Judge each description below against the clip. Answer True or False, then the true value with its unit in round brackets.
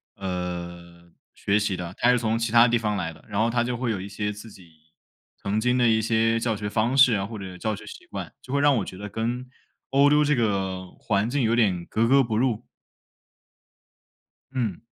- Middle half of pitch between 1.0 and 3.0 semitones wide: False (3.6 semitones)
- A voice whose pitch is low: True (110 Hz)